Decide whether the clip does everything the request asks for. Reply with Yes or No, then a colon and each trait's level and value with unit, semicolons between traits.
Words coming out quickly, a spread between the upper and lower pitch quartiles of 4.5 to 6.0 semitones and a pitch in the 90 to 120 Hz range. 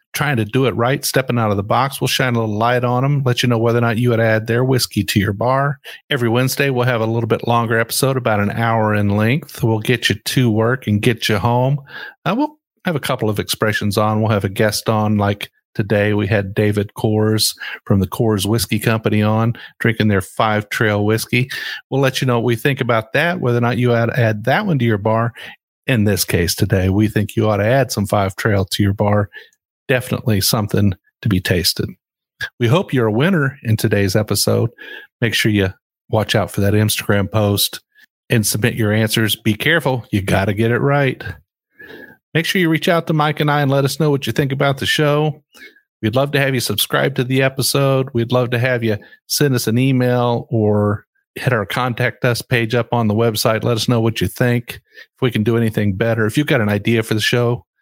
No: fast, 230 wpm; average, 3.5 semitones; low, 115 Hz